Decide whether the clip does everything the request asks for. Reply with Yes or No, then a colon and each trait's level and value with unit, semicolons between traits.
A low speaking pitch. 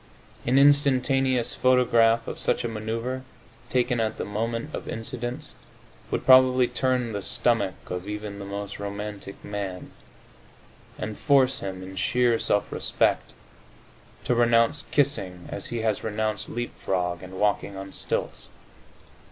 Yes: low, 115 Hz